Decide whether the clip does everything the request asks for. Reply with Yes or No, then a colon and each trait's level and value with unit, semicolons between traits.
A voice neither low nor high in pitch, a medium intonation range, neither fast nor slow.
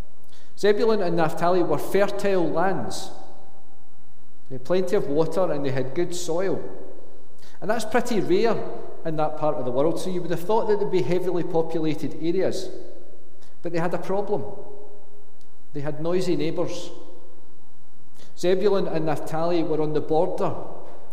Yes: medium, 170 Hz; average, 3.9 semitones; average, 150 wpm